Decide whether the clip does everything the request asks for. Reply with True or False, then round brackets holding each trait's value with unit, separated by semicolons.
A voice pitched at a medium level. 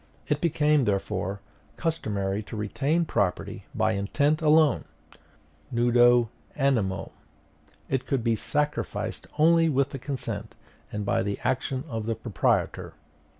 False (120 Hz)